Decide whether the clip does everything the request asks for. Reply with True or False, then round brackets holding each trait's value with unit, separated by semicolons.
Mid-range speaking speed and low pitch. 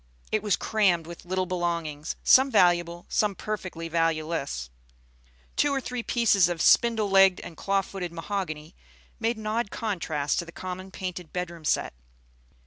False (150 wpm; 180 Hz)